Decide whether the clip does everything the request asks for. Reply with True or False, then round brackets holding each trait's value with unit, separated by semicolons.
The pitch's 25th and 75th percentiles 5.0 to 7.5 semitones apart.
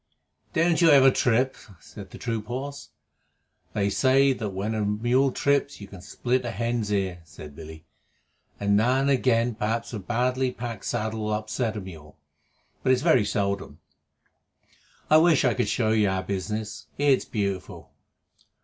False (4.2 semitones)